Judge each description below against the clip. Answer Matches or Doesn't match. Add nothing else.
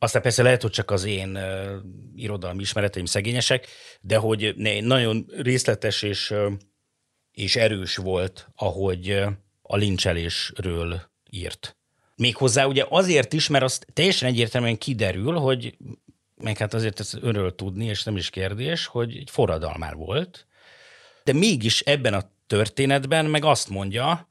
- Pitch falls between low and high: Doesn't match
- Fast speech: Doesn't match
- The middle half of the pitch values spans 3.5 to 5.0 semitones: Matches